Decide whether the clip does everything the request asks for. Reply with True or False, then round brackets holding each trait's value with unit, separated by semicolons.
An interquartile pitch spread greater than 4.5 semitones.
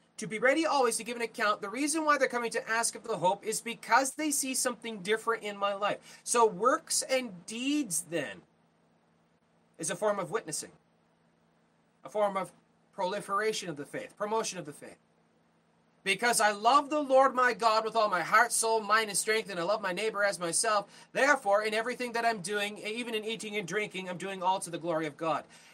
False (4.2 semitones)